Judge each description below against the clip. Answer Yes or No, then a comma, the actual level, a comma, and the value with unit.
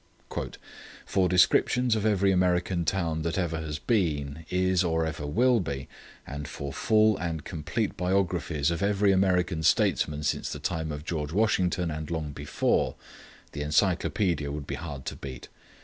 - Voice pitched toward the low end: Yes, very low, 85 Hz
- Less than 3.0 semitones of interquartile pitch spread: No, average, 4.0 semitones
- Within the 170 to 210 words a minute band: No, average, 155 wpm